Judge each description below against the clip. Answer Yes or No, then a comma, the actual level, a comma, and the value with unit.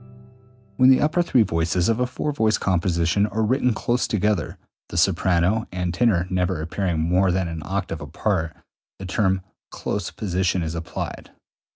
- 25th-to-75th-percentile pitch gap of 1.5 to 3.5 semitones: No, average, 4.2 semitones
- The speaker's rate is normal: Yes, average, 160 wpm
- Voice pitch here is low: Yes, very low, 95 Hz